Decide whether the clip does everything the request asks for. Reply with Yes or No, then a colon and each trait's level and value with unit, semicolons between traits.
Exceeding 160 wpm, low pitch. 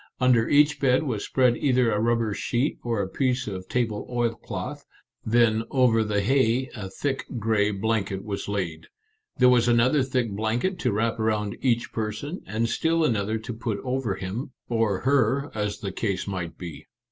Yes: average, 170 wpm; low, 115 Hz